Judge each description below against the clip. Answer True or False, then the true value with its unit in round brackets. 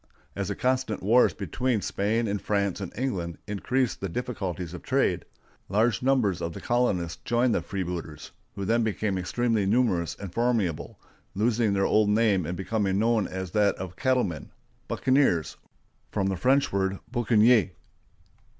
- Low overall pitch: True (105 Hz)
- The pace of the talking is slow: False (150 wpm)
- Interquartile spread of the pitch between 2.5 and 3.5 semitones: False (4.1 semitones)